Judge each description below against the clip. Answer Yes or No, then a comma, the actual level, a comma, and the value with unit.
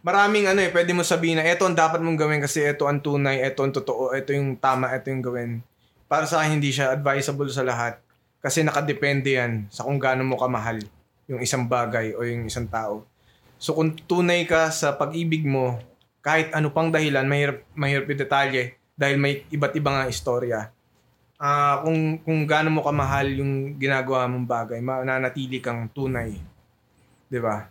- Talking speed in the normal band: No, fast, 180 wpm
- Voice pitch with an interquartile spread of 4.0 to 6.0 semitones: No, average, 3.1 semitones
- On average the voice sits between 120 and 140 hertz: Yes, low, 135 Hz